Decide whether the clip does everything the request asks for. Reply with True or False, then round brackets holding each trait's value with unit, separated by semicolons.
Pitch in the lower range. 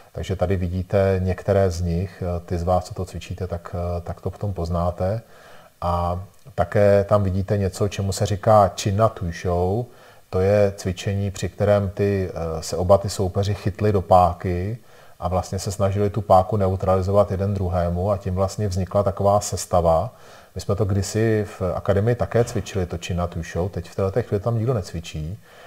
True (95 Hz)